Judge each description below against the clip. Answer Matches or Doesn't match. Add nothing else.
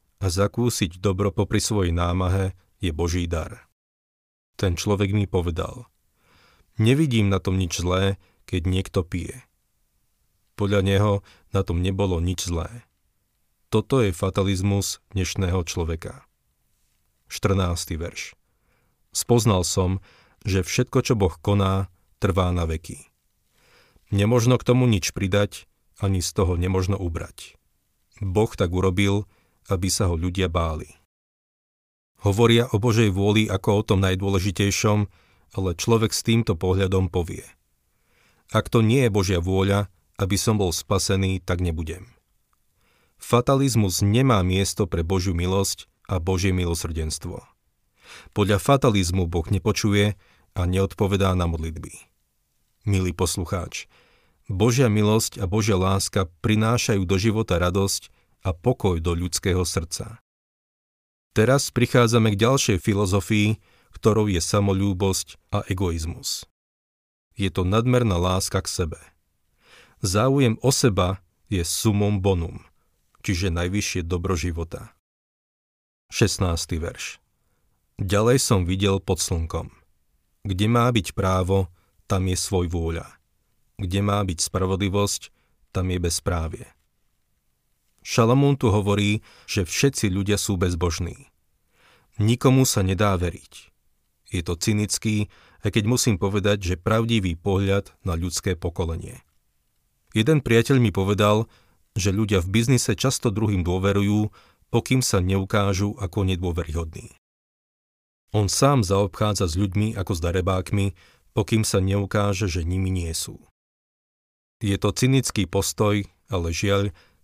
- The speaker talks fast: Doesn't match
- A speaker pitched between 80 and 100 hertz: Matches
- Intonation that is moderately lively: Matches